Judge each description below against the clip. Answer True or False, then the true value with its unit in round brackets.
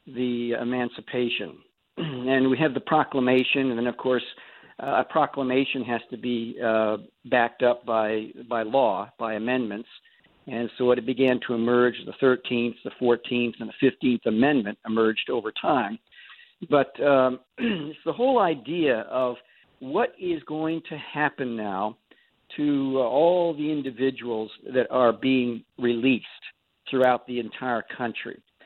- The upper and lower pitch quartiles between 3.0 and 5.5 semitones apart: False (2.4 semitones)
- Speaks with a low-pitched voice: True (125 Hz)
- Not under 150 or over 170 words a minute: False (140 wpm)